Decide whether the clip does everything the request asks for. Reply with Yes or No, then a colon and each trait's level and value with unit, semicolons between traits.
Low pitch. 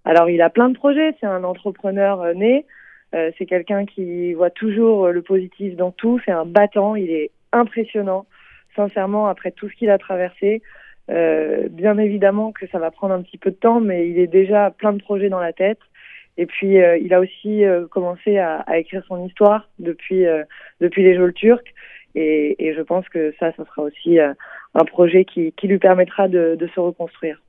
No: medium, 185 Hz